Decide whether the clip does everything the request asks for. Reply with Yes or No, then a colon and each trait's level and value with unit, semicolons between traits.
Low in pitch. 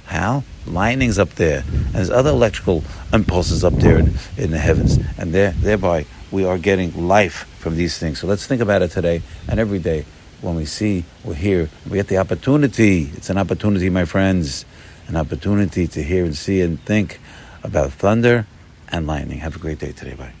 Yes: very low, 90 Hz